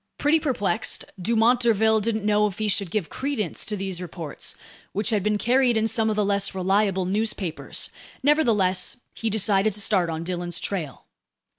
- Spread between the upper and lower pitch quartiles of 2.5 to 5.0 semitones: Yes, average, 2.9 semitones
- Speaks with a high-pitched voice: Yes, high, 210 Hz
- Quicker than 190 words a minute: No, average, 170 wpm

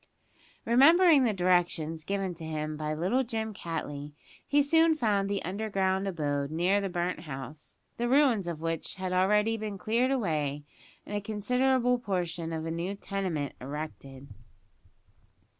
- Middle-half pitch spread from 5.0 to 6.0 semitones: Yes, wide, 5.5 semitones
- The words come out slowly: No, average, 145 wpm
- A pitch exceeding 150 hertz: Yes, high, 190 Hz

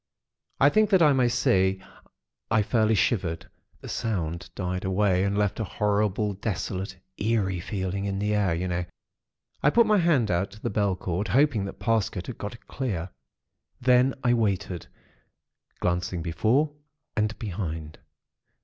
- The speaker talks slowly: No, average, 155 wpm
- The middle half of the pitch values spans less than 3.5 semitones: No, average, 4.0 semitones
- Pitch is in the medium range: No, low, 100 Hz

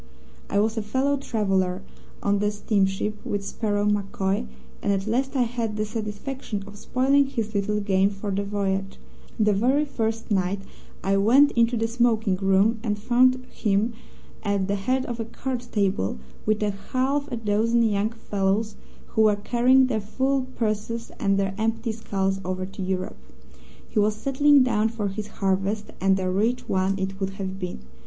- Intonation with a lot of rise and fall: No, average, 3.0 semitones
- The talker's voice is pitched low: No, high, 210 Hz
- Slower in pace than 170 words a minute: No, average, 175 wpm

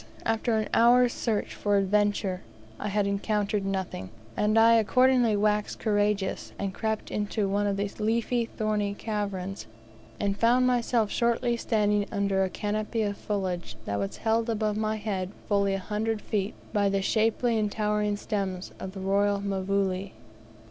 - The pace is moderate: Yes, average, 155 wpm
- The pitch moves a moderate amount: No, narrow, 1.8 semitones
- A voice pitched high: Yes, high, 210 Hz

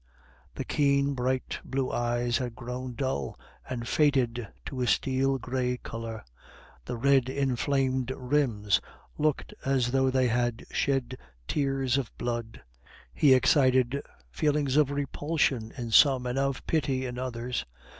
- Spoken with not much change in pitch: Yes, narrow, 2.1 semitones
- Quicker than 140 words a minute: No, slow, 135 wpm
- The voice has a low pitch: Yes, low, 130 Hz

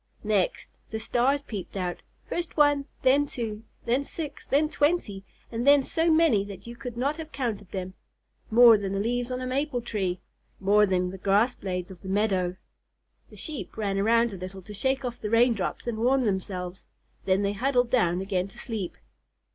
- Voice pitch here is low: No, high, 225 Hz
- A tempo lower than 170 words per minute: No, average, 190 wpm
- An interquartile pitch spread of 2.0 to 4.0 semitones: No, average, 5.1 semitones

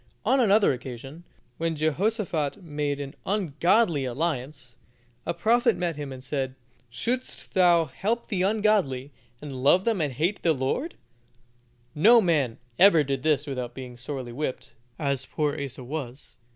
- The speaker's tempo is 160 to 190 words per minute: No, average, 145 wpm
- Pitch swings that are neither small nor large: No, wide, 5.8 semitones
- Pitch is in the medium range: Yes, medium, 150 Hz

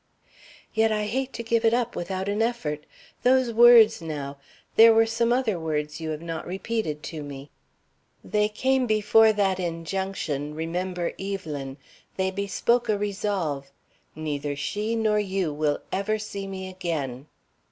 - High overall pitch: Yes, high, 195 Hz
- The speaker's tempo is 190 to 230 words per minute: No, average, 150 wpm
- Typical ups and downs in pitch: No, wide, 6.0 semitones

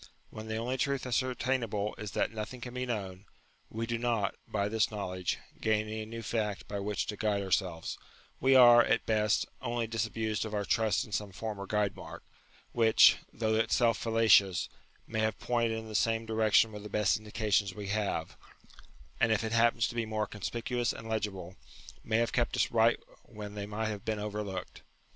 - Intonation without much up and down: Yes, narrow, 1.8 semitones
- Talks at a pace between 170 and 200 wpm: Yes, average, 190 wpm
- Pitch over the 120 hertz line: No, low, 110 Hz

